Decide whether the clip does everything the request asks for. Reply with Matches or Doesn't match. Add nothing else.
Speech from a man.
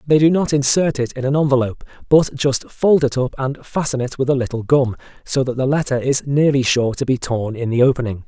Matches